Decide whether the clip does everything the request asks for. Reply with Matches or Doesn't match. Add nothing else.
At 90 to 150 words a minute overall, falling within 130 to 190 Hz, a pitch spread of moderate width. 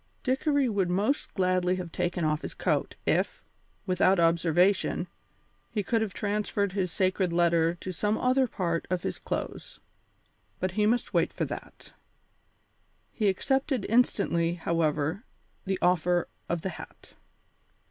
Matches